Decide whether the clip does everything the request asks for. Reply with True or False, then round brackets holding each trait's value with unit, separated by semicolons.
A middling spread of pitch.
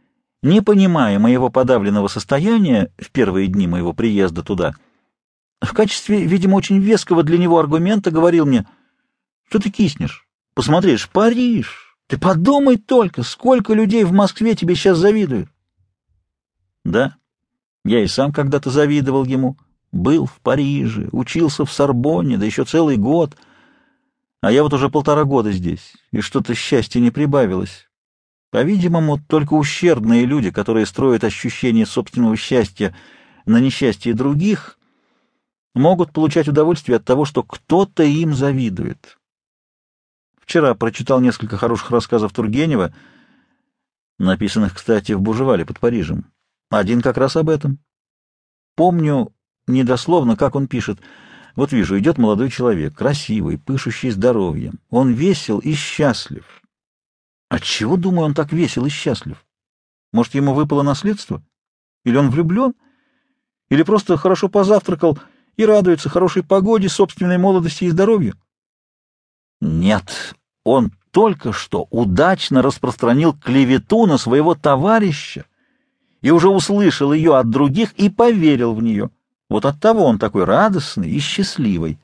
False (8.1 semitones)